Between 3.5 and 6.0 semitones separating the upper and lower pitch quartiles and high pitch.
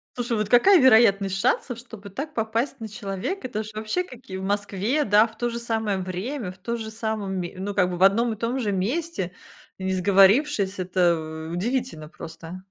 Yes: average, 4.0 semitones; high, 210 Hz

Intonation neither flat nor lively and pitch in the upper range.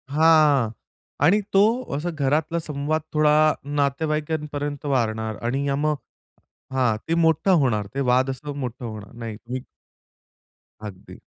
No: average, 3.8 semitones; medium, 140 Hz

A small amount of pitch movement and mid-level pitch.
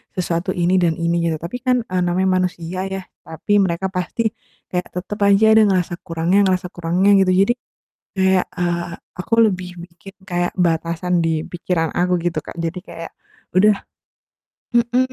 Yes: narrow, 1.9 semitones; medium, 180 Hz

